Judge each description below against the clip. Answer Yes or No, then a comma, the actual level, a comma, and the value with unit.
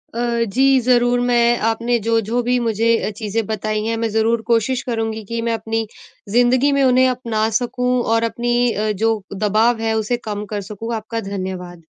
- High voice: Yes, high, 230 Hz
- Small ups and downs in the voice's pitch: Yes, narrow, 1.9 semitones